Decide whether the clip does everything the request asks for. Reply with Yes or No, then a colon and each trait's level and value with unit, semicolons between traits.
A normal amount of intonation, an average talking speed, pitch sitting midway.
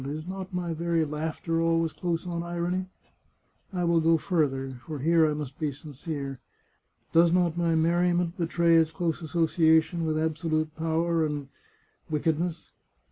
No: narrow, 1.6 semitones; average, 160 wpm; medium, 165 Hz